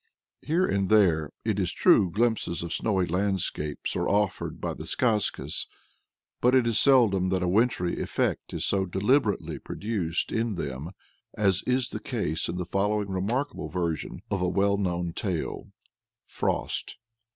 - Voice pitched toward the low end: Yes, low, 100 Hz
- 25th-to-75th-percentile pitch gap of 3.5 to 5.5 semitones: Yes, average, 3.9 semitones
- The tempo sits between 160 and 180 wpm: No, average, 150 wpm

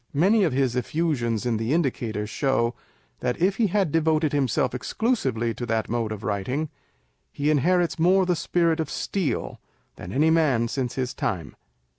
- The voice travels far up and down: Yes, wide, 5.9 semitones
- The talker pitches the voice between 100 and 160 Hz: Yes, medium, 140 Hz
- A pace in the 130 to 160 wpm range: No, average, 170 wpm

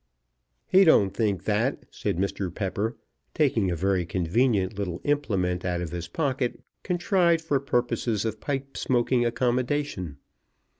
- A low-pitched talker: Yes, low, 110 Hz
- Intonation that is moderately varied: No, wide, 6.5 semitones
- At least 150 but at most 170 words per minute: No, slow, 135 wpm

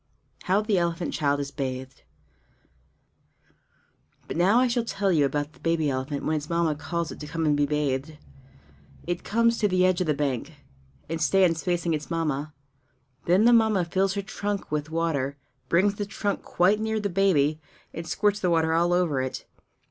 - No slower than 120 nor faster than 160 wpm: No, average, 185 wpm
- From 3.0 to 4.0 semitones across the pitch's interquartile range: No, average, 4.7 semitones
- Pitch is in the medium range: Yes, medium, 170 Hz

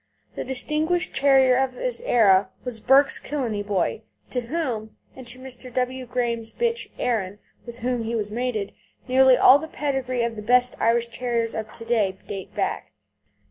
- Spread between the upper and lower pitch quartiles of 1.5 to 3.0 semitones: Yes, average, 2.7 semitones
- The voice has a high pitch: Yes, high, 245 Hz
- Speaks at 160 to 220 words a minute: Yes, average, 170 wpm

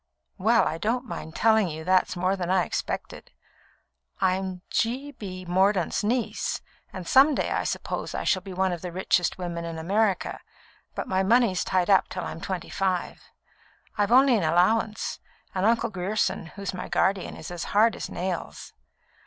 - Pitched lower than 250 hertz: Yes, high, 190 Hz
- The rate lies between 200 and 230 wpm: No, average, 170 wpm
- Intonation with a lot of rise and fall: No, average, 3.4 semitones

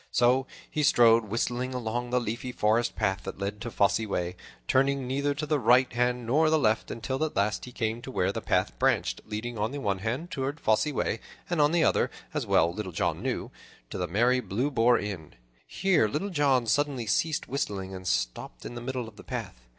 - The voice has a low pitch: Yes, low, 120 Hz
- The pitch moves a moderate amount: Yes, average, 4.3 semitones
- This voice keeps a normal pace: No, fast, 215 wpm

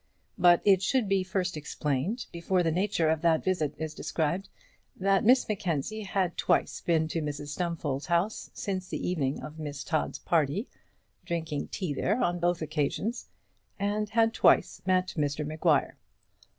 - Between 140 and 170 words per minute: Yes, average, 155 wpm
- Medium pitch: Yes, medium, 170 Hz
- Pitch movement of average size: Yes, average, 4.0 semitones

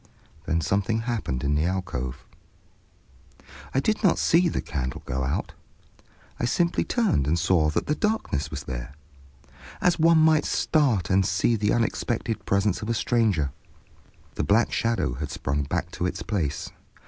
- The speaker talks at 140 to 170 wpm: Yes, average, 160 wpm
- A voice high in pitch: No, low, 100 Hz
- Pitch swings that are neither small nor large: No, wide, 8.4 semitones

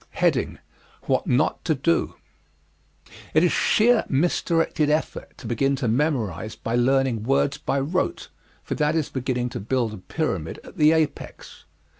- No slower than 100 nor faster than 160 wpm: Yes, average, 145 wpm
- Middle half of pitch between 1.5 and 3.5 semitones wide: No, average, 4.6 semitones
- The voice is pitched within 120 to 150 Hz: Yes, low, 135 Hz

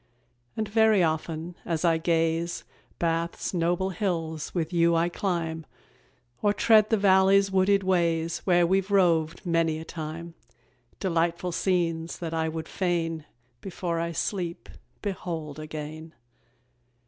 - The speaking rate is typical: No, slow, 125 wpm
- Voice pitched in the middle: Yes, medium, 170 Hz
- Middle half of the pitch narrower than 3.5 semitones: Yes, narrow, 2.5 semitones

